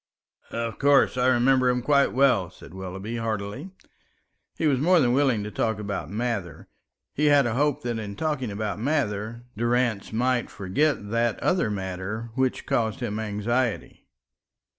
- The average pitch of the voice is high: No, low, 115 Hz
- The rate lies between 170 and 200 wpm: No, average, 155 wpm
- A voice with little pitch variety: No, average, 3.9 semitones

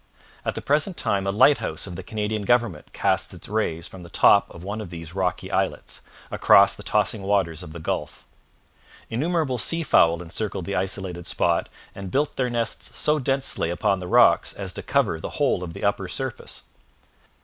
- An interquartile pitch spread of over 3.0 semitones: Yes, average, 4.9 semitones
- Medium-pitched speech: No, low, 100 Hz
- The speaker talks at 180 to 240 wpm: Yes, average, 185 wpm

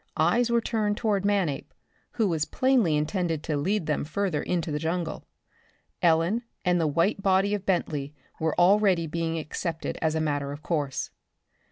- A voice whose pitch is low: No, medium, 170 Hz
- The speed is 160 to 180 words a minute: Yes, average, 165 wpm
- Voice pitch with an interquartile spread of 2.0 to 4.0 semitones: No, average, 4.4 semitones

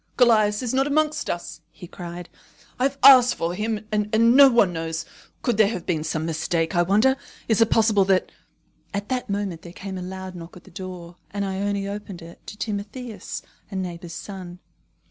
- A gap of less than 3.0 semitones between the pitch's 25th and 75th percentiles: No, average, 4.0 semitones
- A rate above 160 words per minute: Yes, average, 195 wpm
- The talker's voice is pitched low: No, high, 200 Hz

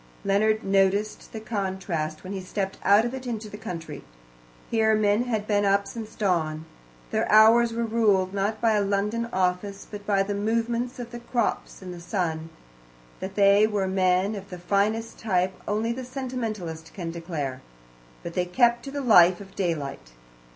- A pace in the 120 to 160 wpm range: No, average, 175 wpm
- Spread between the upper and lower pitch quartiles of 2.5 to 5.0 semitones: Yes, average, 3.3 semitones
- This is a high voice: Yes, high, 200 Hz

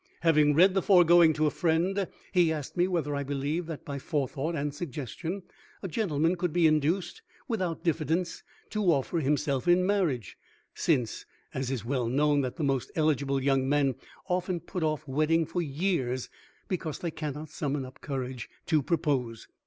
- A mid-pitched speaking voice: Yes, medium, 155 Hz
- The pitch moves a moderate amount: Yes, average, 3.9 semitones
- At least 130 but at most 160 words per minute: No, average, 170 wpm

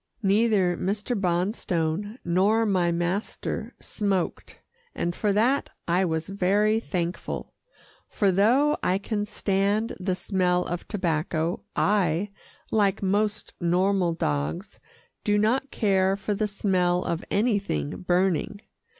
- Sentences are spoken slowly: Yes, slow, 115 wpm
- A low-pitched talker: No, high, 195 Hz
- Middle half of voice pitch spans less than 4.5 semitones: Yes, average, 2.8 semitones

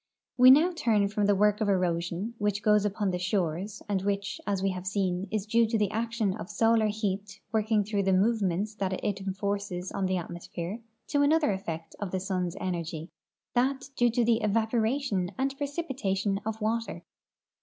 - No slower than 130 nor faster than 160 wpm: No, average, 185 wpm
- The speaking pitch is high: Yes, high, 205 Hz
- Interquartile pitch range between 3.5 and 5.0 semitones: No, average, 3.0 semitones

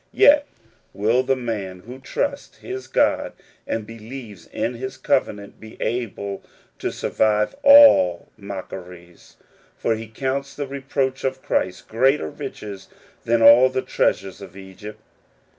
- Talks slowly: Yes, slow, 130 wpm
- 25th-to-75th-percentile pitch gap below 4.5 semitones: No, average, 4.9 semitones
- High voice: No, low, 115 Hz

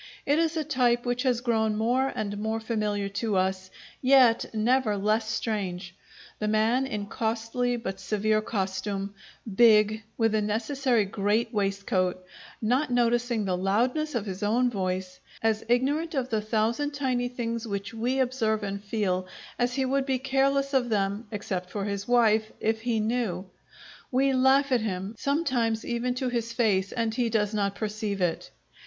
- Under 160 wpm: No, average, 165 wpm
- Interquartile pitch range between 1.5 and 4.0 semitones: Yes, average, 3.4 semitones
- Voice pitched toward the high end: Yes, high, 225 Hz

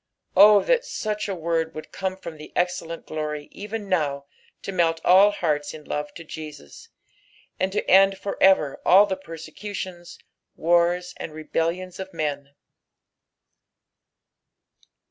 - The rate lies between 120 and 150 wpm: Yes, slow, 135 wpm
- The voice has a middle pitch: Yes, medium, 175 Hz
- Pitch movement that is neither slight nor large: Yes, average, 3.6 semitones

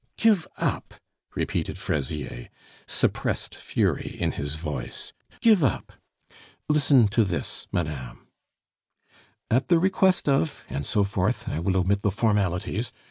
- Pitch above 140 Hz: No, low, 100 Hz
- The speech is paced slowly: Yes, slow, 125 wpm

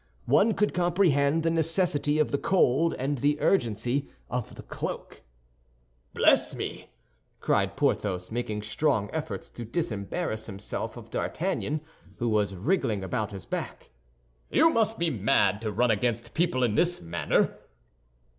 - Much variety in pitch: Yes, wide, 7.4 semitones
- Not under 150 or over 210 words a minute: No, average, 140 wpm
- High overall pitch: No, low, 125 Hz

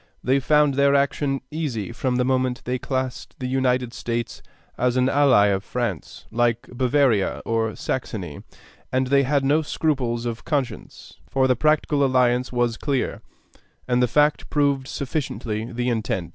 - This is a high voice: No, low, 130 Hz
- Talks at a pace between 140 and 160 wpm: Yes, average, 155 wpm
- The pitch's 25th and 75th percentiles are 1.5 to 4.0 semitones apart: Yes, average, 2.7 semitones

